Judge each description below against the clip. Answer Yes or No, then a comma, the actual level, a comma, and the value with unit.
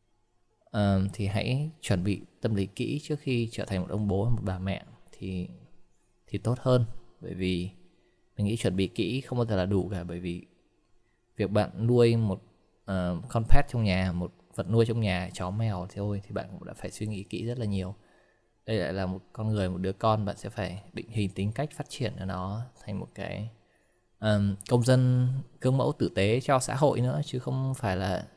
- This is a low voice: Yes, low, 105 Hz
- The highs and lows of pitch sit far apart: No, average, 4.1 semitones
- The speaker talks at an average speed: Yes, average, 220 wpm